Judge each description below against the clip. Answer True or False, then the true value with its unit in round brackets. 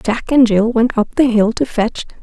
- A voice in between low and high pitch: False (230 Hz)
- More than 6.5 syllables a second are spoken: False (4.4 syllables/s)